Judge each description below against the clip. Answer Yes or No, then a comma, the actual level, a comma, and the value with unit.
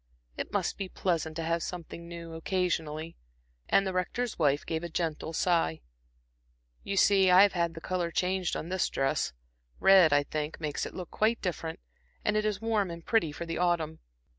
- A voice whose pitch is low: No, medium, 170 Hz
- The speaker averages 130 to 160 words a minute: No, average, 190 wpm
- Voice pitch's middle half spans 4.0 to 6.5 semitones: No, average, 2.7 semitones